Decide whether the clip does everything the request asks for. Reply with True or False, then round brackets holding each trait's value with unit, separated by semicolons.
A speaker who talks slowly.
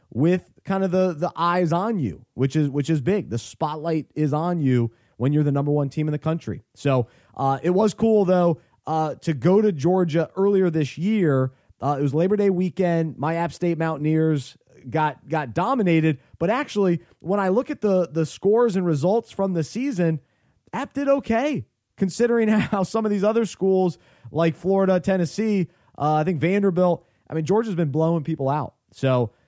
False (190 wpm)